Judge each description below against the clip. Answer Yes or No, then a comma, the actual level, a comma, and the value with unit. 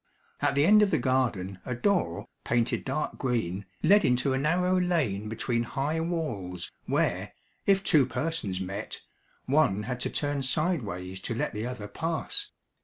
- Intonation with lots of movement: Yes, wide, 7.5 semitones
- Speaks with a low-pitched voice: Yes, low, 130 Hz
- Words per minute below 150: No, average, 160 wpm